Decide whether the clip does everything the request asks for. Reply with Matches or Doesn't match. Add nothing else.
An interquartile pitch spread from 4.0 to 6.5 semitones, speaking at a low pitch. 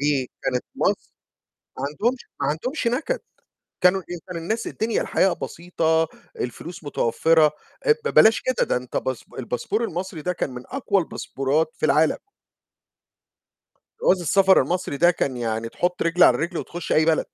Doesn't match